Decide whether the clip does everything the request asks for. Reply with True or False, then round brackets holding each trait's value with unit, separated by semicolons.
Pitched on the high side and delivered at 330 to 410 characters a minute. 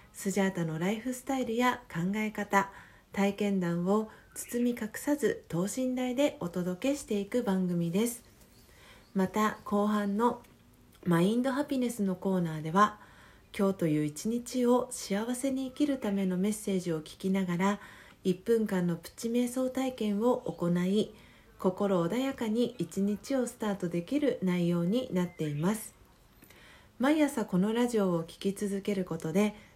False (205 Hz; 285 characters per minute)